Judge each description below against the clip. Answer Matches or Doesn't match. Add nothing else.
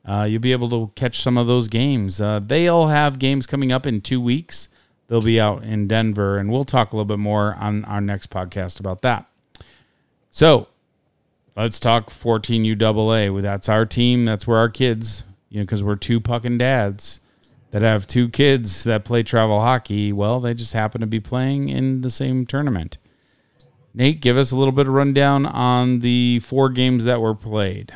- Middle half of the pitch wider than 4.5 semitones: Doesn't match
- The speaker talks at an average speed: Matches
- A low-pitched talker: Matches